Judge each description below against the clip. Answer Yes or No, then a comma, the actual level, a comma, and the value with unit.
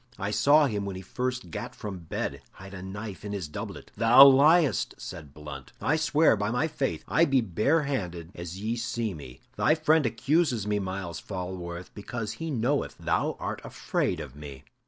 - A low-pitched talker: Yes, low, 105 Hz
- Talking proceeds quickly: No, average, 180 wpm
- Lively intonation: Yes, wide, 7.0 semitones